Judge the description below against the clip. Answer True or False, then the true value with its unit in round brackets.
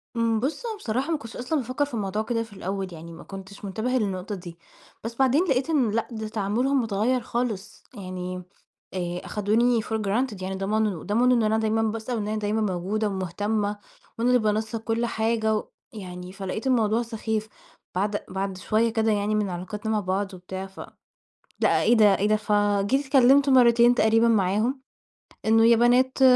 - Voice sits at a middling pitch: False (220 Hz)